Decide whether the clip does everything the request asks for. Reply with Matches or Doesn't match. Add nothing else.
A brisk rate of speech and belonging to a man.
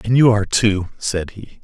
Matches